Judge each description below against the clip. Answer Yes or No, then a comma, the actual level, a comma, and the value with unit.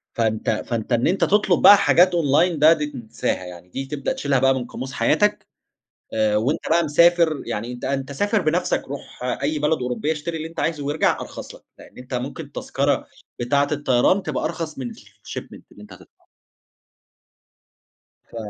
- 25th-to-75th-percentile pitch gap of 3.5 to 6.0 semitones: Yes, average, 4.6 semitones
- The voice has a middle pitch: Yes, medium, 145 Hz